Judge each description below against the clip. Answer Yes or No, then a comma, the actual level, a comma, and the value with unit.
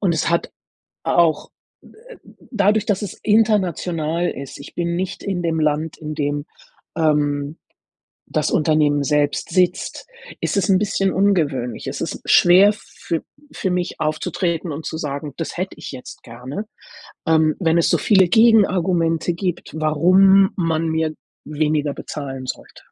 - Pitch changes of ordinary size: Yes, average, 3.6 semitones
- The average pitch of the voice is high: No, medium, 165 Hz